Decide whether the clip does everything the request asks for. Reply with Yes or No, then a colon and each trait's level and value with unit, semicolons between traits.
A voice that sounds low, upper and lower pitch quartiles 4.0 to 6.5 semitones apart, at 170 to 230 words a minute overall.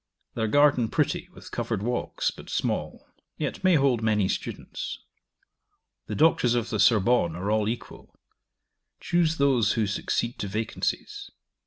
No: low, 115 Hz; average, 4.6 semitones; average, 140 wpm